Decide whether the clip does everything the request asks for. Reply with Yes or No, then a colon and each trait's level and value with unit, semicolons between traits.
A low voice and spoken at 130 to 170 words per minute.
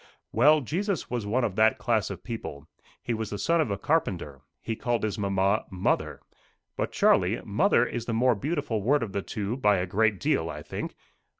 No: low, 110 Hz; average, 200 wpm